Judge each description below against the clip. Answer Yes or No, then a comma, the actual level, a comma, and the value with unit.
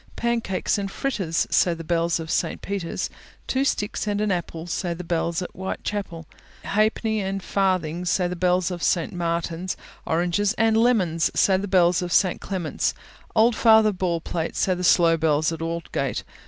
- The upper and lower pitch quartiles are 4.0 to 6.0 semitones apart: No, average, 3.2 semitones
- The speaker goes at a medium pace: Yes, average, 170 wpm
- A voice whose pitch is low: No, medium, 180 Hz